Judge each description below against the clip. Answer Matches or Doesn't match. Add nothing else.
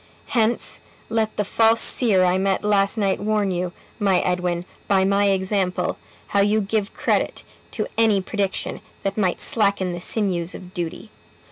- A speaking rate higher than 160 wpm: Doesn't match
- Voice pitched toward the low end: Doesn't match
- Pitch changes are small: Matches